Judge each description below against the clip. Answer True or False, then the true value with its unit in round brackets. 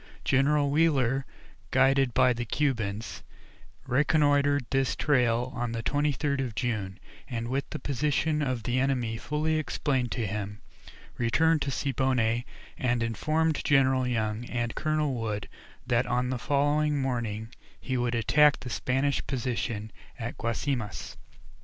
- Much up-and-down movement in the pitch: False (3.4 semitones)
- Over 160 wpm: False (135 wpm)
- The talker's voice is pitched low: True (130 Hz)